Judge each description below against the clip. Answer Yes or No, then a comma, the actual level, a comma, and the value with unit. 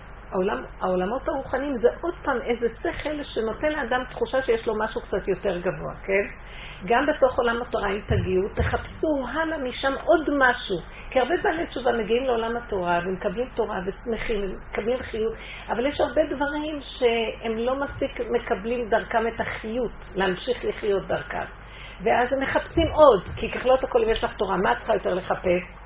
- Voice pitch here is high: Yes, high, 235 Hz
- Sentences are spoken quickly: Yes, fast, 165 wpm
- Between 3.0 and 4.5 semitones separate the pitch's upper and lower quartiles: Yes, average, 3.9 semitones